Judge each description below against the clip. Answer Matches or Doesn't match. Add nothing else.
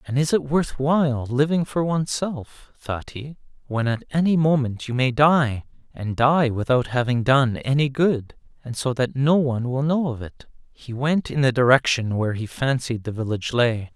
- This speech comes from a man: Matches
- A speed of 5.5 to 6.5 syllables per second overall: Doesn't match